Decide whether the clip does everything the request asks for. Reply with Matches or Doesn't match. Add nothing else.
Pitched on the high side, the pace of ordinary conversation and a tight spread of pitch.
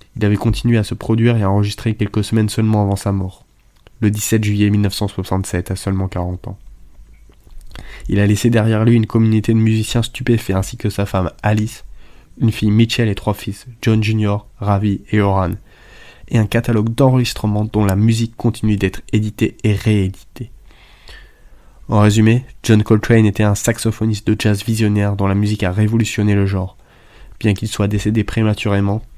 Doesn't match